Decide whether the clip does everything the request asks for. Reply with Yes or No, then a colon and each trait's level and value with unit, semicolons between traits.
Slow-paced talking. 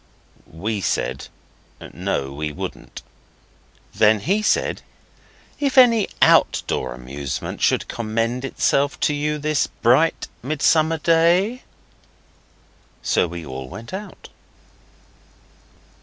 Yes: slow, 100 wpm